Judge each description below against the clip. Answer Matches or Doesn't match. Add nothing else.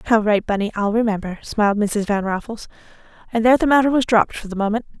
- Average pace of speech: Doesn't match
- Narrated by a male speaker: Doesn't match